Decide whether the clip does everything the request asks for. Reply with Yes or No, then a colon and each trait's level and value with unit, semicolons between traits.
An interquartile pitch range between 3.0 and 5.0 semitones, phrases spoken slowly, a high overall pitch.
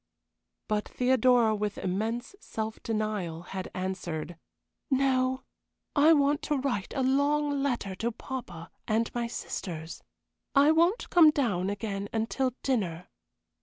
No: wide, 5.6 semitones; slow, 125 wpm; high, 230 Hz